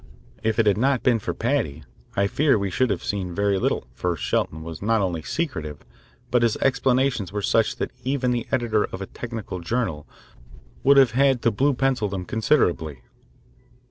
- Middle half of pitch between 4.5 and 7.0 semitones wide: Yes, average, 5.3 semitones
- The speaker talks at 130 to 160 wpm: No, average, 180 wpm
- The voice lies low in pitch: Yes, low, 110 Hz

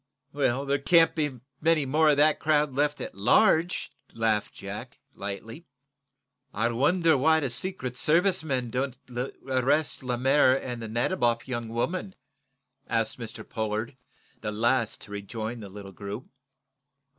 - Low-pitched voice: Yes, low, 130 Hz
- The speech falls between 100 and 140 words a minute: Yes, slow, 135 wpm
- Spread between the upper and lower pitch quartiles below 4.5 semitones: No, average, 4.8 semitones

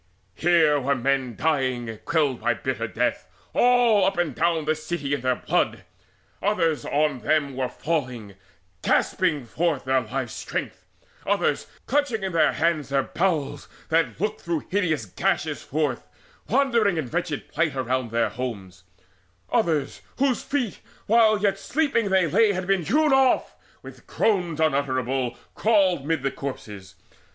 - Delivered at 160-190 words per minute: No, average, 145 wpm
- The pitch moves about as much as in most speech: No, wide, 6.6 semitones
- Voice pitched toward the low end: No, medium, 155 Hz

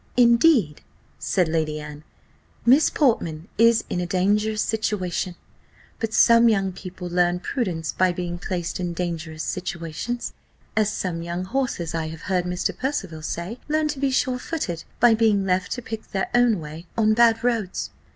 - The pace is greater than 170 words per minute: No, average, 160 wpm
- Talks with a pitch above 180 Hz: Yes, high, 190 Hz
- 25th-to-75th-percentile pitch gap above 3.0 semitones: Yes, average, 5.2 semitones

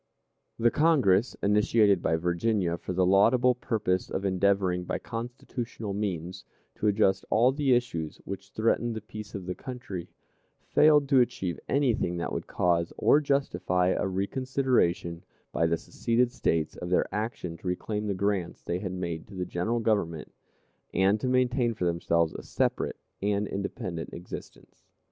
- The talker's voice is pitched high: No, low, 100 Hz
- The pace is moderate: Yes, average, 155 wpm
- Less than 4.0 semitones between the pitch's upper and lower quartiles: No, average, 4.8 semitones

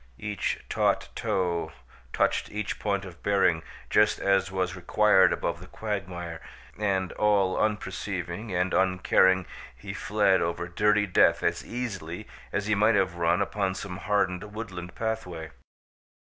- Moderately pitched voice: No, very low, 95 Hz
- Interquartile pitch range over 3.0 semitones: No, average, 2.7 semitones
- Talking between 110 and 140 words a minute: Yes, slow, 135 wpm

